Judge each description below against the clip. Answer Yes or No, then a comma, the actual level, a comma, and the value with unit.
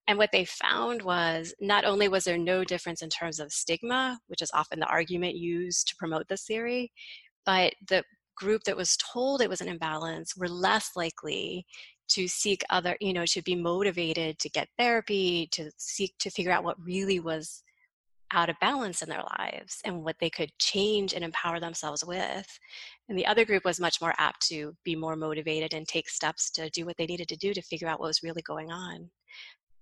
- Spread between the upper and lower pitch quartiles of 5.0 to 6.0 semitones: No, average, 3.1 semitones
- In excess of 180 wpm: Yes, fast, 205 wpm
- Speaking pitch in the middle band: Yes, medium, 175 Hz